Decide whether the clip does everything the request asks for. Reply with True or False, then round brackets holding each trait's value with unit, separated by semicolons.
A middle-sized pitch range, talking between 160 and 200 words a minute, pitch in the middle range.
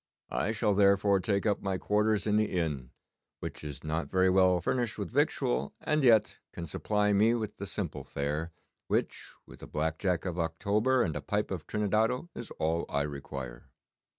False (5.0 semitones; 180 wpm; 95 Hz)